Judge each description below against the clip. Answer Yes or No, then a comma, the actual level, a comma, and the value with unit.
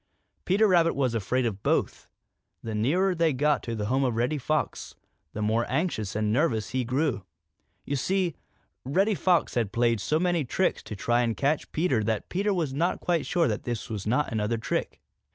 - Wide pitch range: Yes, wide, 6.7 semitones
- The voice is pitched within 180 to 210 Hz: No, low, 130 Hz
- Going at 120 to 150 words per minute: No, average, 190 wpm